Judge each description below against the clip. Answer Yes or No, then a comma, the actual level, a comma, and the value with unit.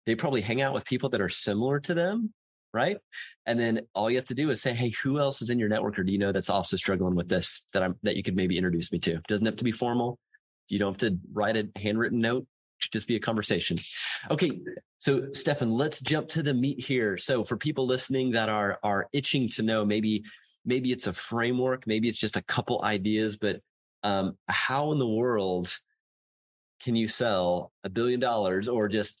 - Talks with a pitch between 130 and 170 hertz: No, low, 115 Hz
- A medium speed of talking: No, fast, 225 wpm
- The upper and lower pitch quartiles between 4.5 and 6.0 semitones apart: No, average, 3.6 semitones